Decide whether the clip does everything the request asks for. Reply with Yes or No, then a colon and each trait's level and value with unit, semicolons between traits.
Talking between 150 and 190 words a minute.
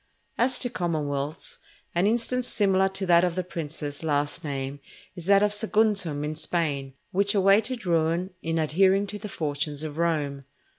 Yes: average, 160 wpm